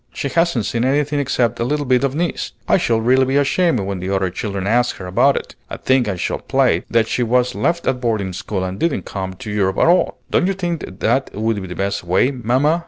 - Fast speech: Yes, fast, 240 wpm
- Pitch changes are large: Yes, wide, 6.0 semitones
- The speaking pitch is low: Yes, low, 120 Hz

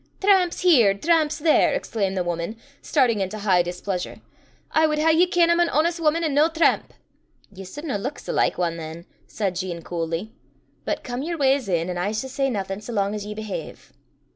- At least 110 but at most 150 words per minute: No, average, 200 wpm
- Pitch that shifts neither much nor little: No, wide, 8.7 semitones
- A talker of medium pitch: No, high, 220 Hz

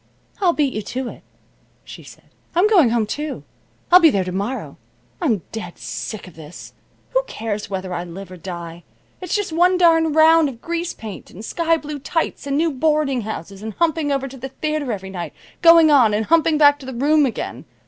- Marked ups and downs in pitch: Yes, wide, 7.6 semitones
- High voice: Yes, very high, 275 Hz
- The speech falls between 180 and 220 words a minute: Yes, fast, 205 wpm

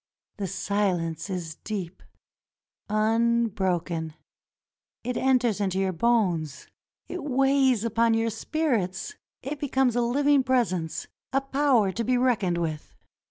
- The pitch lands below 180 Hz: No, high, 225 Hz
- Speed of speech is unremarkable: No, slow, 120 wpm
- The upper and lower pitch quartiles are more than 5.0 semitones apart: Yes, wide, 5.5 semitones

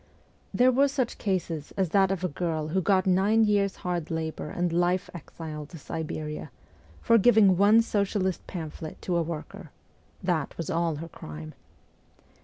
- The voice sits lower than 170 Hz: No, medium, 180 Hz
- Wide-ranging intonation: No, average, 3.7 semitones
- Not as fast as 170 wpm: Yes, average, 160 wpm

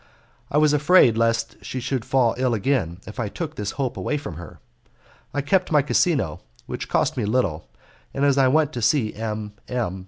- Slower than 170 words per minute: No, average, 195 wpm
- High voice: No, low, 125 Hz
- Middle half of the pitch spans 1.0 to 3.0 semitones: No, average, 5.0 semitones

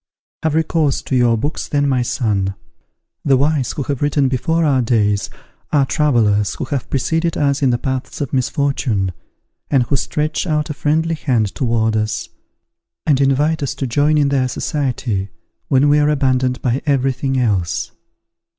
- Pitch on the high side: No, low, 135 Hz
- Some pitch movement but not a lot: Yes, average, 3.5 semitones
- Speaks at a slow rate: No, average, 170 wpm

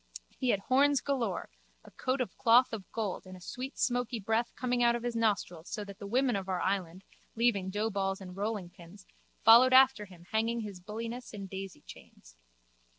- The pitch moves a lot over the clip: No, average, 3.9 semitones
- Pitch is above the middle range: Yes, high, 215 Hz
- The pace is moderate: Yes, average, 180 wpm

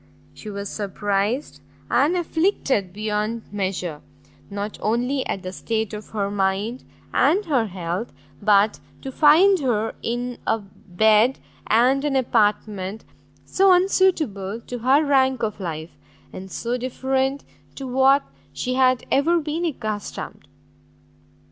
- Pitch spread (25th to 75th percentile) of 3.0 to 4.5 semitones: No, average, 4.9 semitones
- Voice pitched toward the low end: No, high, 230 Hz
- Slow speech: Yes, slow, 125 wpm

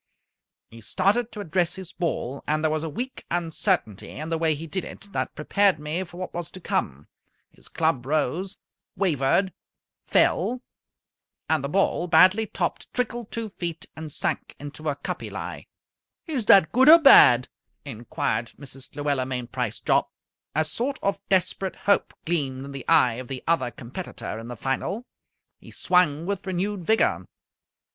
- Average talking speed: Yes, average, 165 wpm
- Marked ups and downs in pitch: Yes, wide, 5.9 semitones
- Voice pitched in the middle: Yes, medium, 165 Hz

